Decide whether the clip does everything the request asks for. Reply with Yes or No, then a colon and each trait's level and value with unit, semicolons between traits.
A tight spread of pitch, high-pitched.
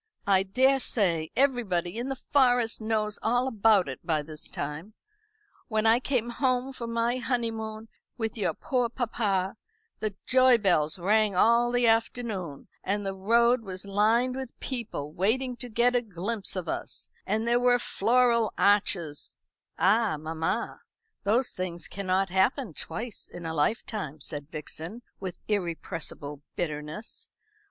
No: average, 4.7 semitones; high, 215 Hz